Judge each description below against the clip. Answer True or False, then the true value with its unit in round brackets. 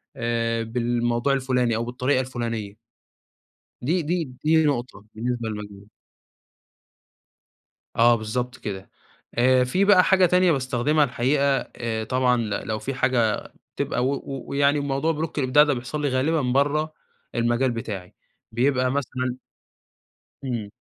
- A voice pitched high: False (125 Hz)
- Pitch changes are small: False (3.3 semitones)